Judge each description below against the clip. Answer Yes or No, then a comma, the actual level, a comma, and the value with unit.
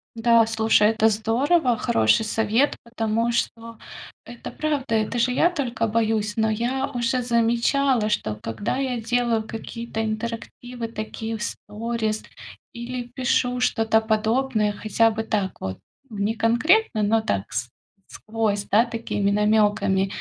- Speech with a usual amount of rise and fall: No, narrow, 1.9 semitones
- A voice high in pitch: Yes, high, 225 Hz